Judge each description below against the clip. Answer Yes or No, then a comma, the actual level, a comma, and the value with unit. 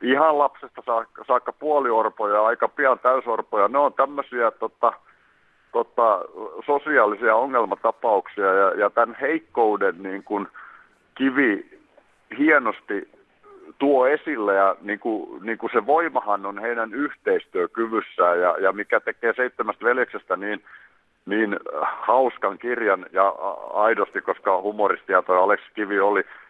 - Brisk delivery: No, average, 120 wpm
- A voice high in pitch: Yes, very high, 375 Hz